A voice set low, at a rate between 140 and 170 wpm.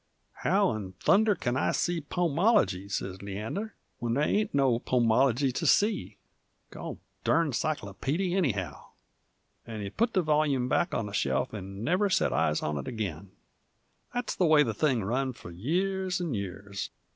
Yes: low, 130 Hz; average, 165 wpm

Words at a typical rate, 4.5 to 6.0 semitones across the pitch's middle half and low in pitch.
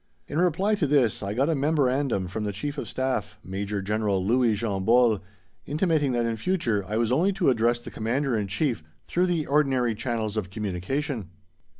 Yes: average, 190 wpm; wide, 5.5 semitones; low, 120 Hz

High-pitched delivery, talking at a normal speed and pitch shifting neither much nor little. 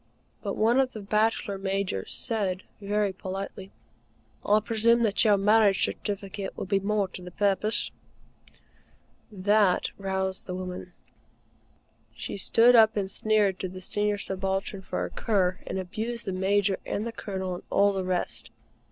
No: high, 200 Hz; average, 150 wpm; narrow, 2.0 semitones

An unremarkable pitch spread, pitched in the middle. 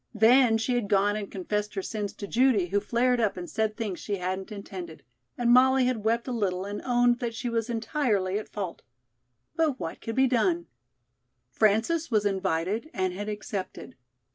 No: average, 3.6 semitones; high, 215 Hz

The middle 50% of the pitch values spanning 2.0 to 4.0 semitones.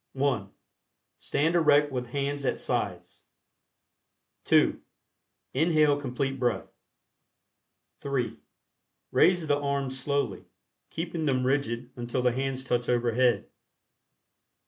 Yes: narrow, 2.6 semitones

